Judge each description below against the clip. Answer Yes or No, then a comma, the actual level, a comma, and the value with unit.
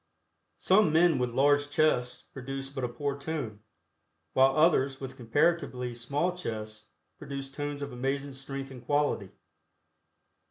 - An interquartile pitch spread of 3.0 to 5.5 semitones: No, narrow, 2.5 semitones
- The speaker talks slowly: Yes, slow, 130 wpm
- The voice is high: No, low, 135 Hz